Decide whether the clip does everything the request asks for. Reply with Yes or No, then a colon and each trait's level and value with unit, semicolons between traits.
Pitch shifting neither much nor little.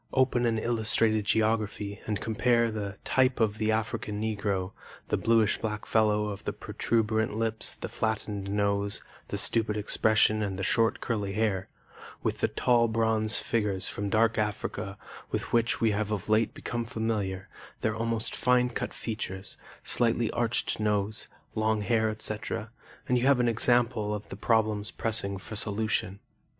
No: narrow, 1.6 semitones